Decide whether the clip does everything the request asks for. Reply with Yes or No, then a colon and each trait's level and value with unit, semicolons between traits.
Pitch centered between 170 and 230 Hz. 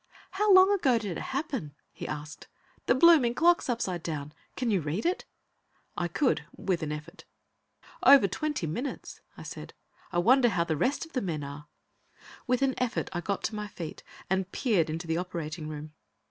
Yes: high, 190 Hz